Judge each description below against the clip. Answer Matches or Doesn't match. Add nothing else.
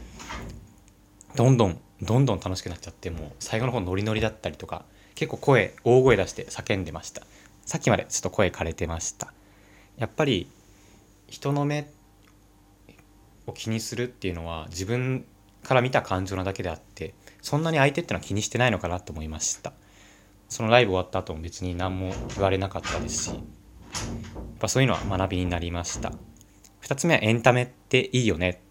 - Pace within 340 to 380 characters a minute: Matches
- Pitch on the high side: Doesn't match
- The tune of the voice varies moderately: Matches